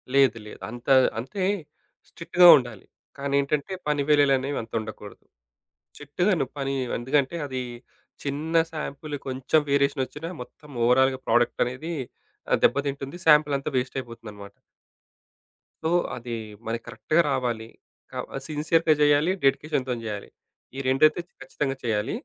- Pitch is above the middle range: No, low, 135 Hz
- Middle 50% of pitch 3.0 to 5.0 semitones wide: Yes, average, 3.3 semitones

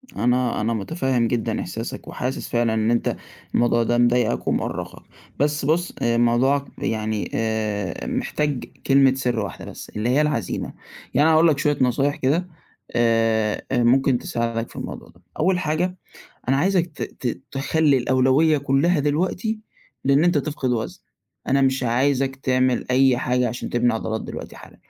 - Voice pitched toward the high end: No, low, 130 Hz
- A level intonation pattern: No, average, 3.6 semitones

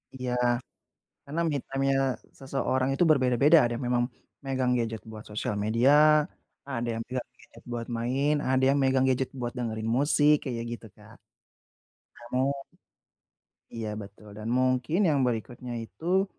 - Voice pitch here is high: No, low, 130 Hz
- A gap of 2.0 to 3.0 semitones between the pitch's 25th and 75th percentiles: Yes, average, 2.7 semitones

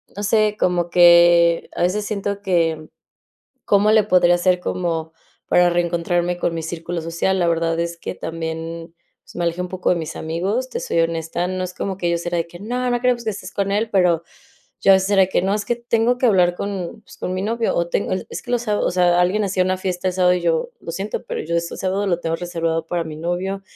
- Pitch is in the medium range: Yes, medium, 180 Hz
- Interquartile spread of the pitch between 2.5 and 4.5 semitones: Yes, average, 2.8 semitones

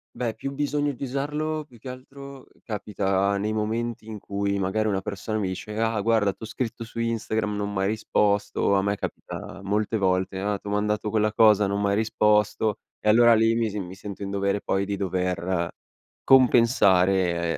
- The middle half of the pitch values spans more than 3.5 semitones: No, narrow, 2.6 semitones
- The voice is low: Yes, low, 105 Hz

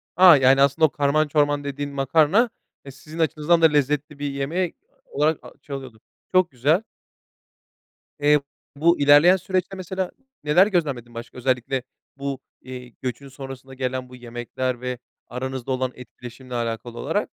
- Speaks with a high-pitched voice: No, medium, 140 Hz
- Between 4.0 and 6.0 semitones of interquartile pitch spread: No, average, 3.3 semitones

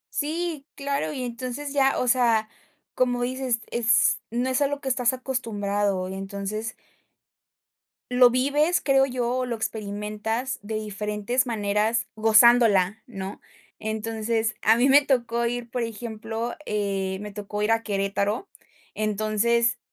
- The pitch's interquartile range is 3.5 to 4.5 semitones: No, average, 3.1 semitones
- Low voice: No, high, 230 Hz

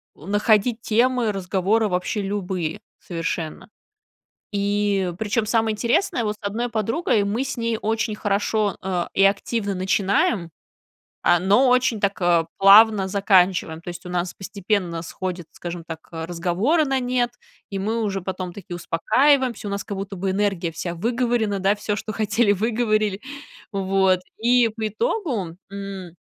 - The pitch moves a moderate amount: Yes, average, 3.2 semitones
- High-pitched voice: Yes, high, 200 Hz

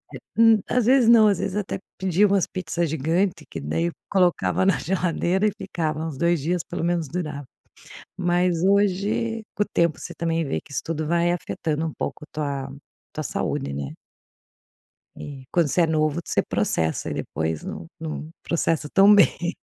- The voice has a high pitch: No, medium, 170 Hz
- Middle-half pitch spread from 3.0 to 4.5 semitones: Yes, average, 3.6 semitones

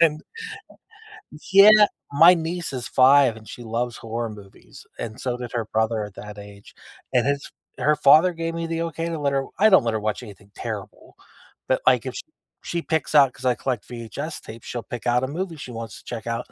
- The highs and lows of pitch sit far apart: Yes, wide, 5.9 semitones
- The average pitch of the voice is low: Yes, low, 125 Hz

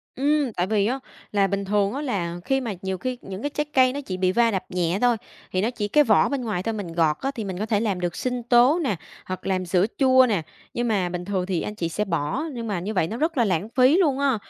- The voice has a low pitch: No, high, 210 Hz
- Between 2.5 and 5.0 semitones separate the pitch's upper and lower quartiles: No, wide, 5.4 semitones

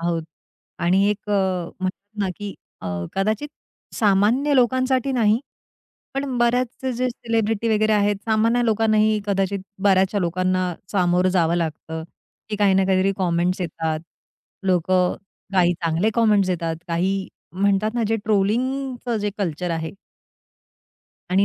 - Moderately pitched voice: No, high, 200 Hz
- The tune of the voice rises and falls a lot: No, average, 3.5 semitones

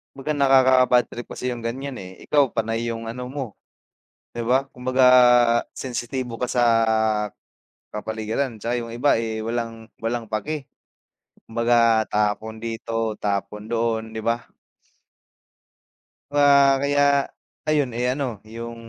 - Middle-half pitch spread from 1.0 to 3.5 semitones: Yes, average, 2.7 semitones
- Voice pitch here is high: No, low, 120 Hz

